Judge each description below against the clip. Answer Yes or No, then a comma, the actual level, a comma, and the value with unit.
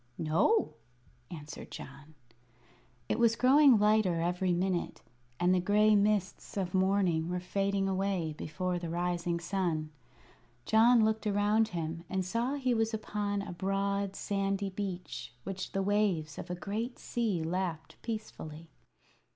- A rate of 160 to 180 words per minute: No, slow, 135 wpm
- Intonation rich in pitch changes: No, average, 3.3 semitones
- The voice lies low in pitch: No, high, 195 Hz